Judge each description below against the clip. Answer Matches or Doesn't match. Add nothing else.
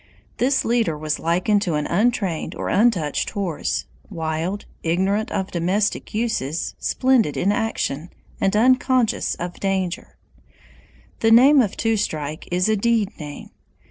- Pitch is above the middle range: Matches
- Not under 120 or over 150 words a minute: Matches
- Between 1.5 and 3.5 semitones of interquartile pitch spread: Doesn't match